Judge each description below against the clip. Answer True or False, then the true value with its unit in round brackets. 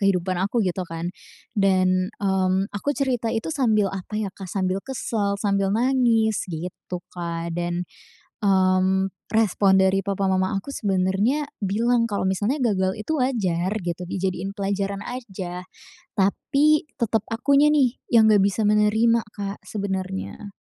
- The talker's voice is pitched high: True (200 Hz)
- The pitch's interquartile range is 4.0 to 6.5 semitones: False (3.1 semitones)